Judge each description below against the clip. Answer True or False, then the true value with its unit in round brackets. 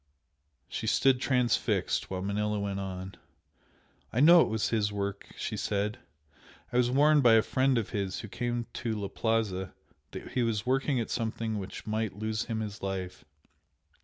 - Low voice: True (110 Hz)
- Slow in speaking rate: False (170 wpm)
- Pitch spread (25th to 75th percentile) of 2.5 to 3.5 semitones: True (3.2 semitones)